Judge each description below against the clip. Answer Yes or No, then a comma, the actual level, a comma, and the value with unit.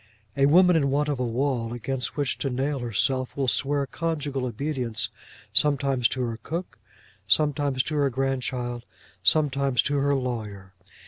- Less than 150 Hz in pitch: Yes, low, 135 Hz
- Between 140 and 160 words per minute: Yes, average, 150 wpm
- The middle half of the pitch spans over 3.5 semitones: No, narrow, 2.6 semitones